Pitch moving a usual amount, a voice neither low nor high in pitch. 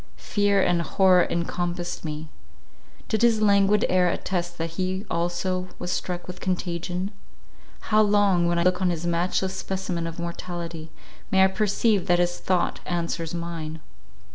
No: narrow, 1.9 semitones; medium, 180 Hz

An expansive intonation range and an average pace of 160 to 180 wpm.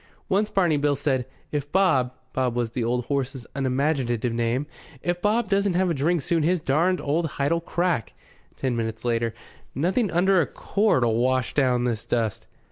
Yes: wide, 6.1 semitones; average, 170 wpm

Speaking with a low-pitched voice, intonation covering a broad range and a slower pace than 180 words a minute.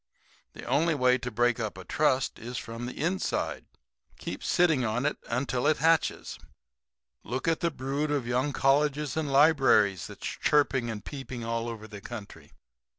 No: low, 130 Hz; average, 4.0 semitones; average, 165 wpm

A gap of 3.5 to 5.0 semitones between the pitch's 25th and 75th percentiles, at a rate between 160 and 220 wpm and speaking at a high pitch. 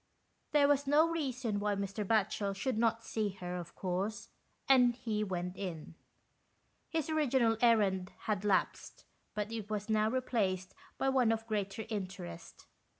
No: average, 3.9 semitones; average, 150 wpm; high, 215 Hz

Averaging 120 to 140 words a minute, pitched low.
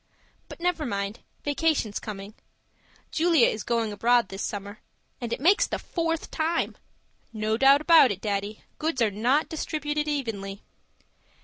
No: slow, 135 wpm; high, 240 Hz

